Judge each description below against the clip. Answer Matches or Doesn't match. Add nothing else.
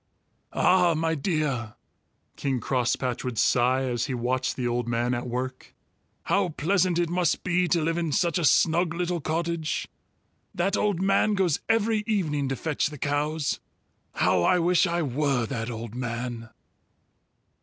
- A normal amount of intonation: Doesn't match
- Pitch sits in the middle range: Matches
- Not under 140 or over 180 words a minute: Matches